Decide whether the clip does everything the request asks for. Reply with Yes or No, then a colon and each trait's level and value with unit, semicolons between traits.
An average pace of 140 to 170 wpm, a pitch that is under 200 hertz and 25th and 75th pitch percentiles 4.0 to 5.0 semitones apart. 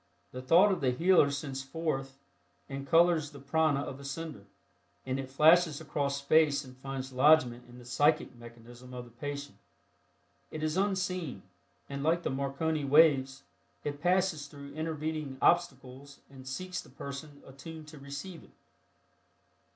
No: average, 150 wpm; medium, 140 Hz; average, 3.0 semitones